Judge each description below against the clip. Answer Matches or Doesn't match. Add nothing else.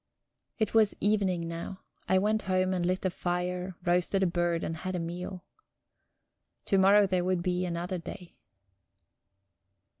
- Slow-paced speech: Doesn't match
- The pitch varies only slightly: Matches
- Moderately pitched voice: Matches